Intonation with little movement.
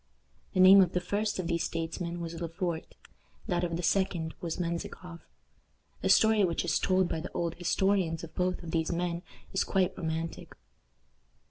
Yes: narrow, 1.9 semitones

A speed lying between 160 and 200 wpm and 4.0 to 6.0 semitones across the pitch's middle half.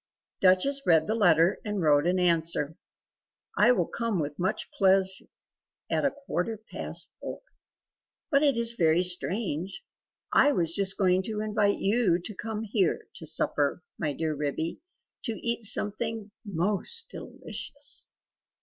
No: average, 140 wpm; average, 5.0 semitones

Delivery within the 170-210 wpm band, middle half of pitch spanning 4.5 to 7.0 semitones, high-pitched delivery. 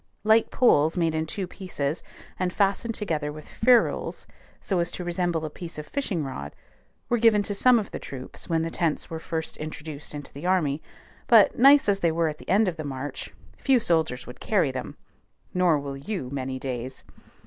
No: average, 195 wpm; average, 5.3 semitones; medium, 165 Hz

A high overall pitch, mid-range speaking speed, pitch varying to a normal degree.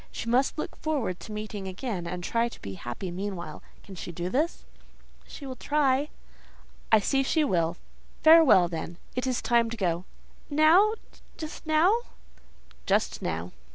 No: high, 225 Hz; average, 155 wpm; wide, 8.5 semitones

